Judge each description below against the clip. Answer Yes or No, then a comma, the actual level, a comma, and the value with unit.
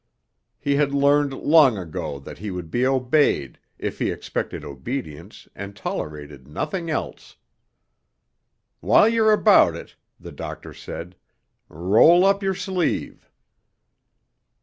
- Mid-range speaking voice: No, low, 130 Hz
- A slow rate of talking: Yes, slow, 120 wpm